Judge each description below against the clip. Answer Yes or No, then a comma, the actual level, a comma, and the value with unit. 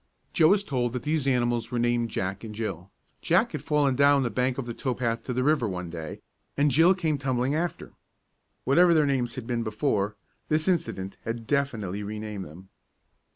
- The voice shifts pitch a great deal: No, average, 4.8 semitones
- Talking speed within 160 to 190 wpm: No, average, 200 wpm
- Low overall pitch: Yes, low, 125 Hz